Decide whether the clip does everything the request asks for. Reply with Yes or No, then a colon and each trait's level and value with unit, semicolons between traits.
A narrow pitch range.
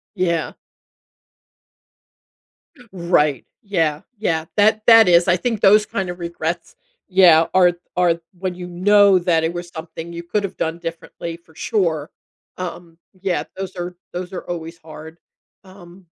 Yes: narrow, 2.1 semitones